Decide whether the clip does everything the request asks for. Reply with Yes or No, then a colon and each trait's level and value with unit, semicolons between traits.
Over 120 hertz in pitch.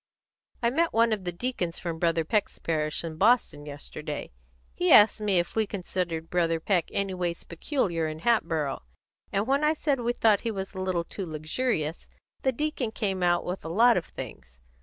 Yes: medium, 185 Hz